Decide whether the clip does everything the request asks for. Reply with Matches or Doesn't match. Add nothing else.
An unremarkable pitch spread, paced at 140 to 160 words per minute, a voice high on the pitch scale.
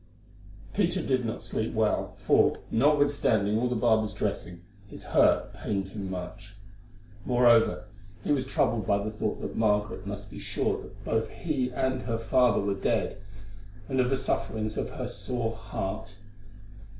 Doesn't match